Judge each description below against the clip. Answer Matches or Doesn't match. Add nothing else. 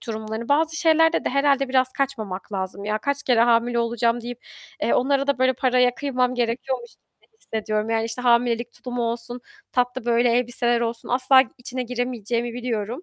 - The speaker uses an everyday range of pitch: Doesn't match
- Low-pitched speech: Doesn't match